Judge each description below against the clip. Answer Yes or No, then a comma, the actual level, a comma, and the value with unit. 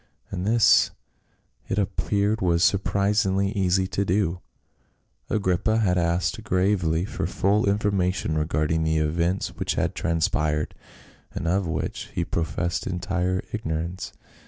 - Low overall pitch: Yes, very low, 90 Hz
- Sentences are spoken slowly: Yes, slow, 125 wpm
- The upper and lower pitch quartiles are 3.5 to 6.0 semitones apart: No, average, 2.9 semitones